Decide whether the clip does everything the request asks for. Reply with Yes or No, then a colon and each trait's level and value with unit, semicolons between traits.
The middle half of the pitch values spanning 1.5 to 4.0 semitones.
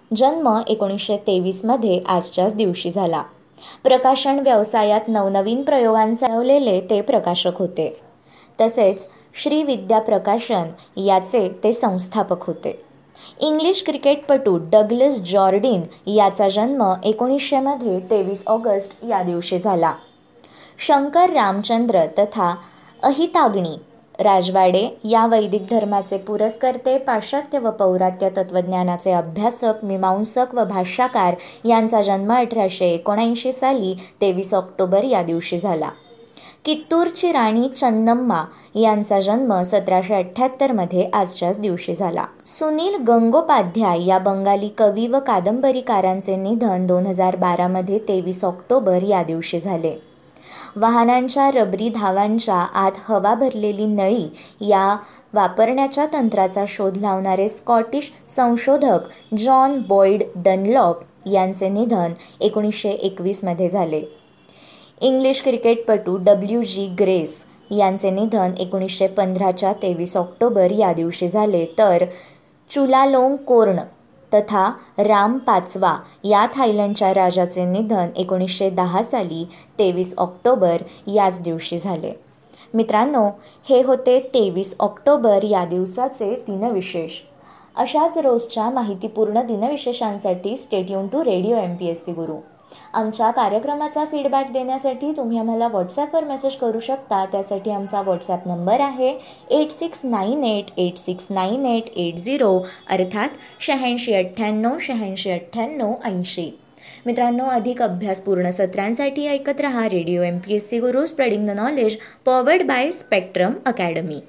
No: average, 4.6 semitones